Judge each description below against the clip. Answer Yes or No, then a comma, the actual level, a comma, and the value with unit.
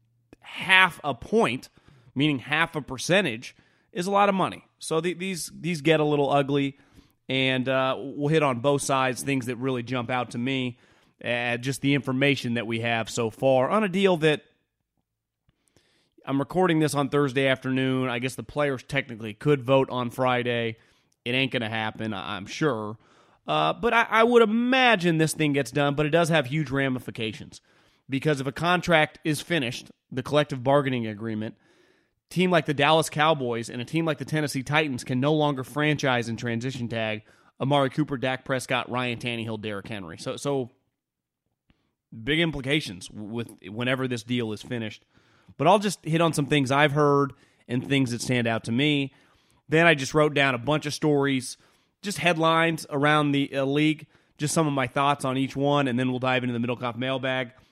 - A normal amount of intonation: Yes, average, 3.7 semitones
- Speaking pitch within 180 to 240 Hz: No, low, 135 Hz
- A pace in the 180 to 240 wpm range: Yes, average, 185 wpm